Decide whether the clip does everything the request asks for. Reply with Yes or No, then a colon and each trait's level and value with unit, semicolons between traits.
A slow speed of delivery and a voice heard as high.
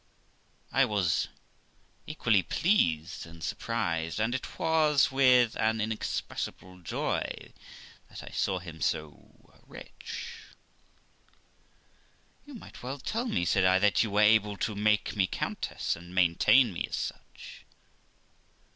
No: slow, 125 wpm; low, 105 Hz